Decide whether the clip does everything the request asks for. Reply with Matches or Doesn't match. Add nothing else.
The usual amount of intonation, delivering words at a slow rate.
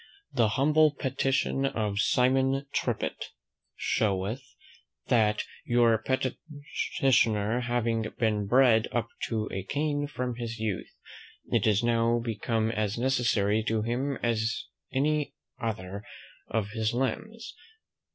Matches